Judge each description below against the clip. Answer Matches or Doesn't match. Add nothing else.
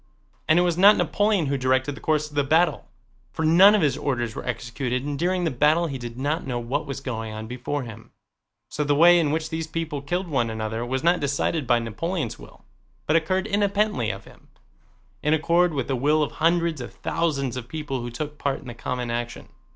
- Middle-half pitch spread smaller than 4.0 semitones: Doesn't match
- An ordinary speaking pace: Doesn't match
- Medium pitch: Matches